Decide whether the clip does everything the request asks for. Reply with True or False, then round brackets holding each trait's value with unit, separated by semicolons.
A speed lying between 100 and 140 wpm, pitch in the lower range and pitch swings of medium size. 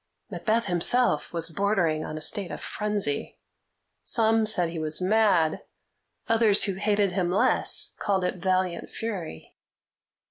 False (135 wpm; 190 Hz; 3.9 semitones)